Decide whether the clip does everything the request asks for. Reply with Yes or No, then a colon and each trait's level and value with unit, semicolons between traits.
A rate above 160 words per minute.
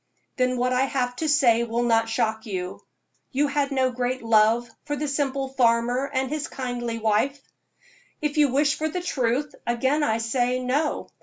Yes: average, 175 wpm